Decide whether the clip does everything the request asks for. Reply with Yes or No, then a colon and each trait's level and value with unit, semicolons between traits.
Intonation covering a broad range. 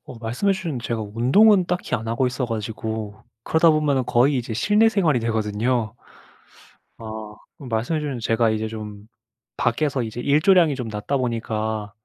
No: average, 4.8 semitones